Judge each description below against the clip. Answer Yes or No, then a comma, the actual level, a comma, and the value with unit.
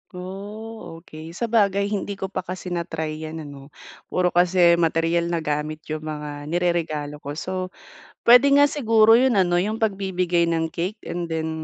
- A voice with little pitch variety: No, average, 3.7 semitones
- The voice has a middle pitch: Yes, medium, 175 Hz